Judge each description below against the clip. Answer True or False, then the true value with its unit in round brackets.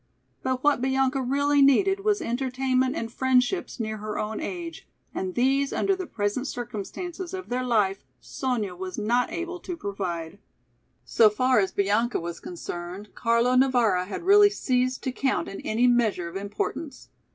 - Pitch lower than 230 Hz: False (250 Hz)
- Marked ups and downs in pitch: False (4.8 semitones)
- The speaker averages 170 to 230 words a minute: False (160 wpm)